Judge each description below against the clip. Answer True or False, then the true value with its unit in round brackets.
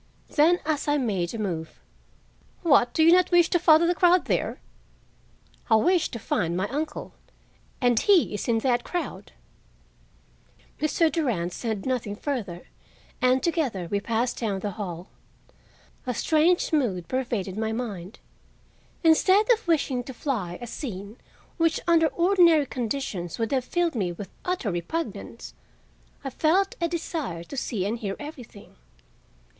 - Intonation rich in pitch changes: True (7.9 semitones)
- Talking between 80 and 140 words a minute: False (150 wpm)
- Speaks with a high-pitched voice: True (255 Hz)